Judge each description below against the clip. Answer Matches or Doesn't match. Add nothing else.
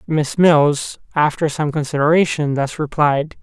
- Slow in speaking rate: Matches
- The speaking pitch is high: Doesn't match